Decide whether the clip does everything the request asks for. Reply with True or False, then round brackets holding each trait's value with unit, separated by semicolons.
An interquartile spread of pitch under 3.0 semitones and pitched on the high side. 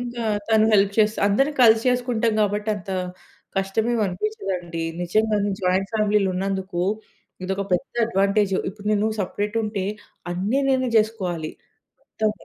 True (2.5 semitones; 210 Hz)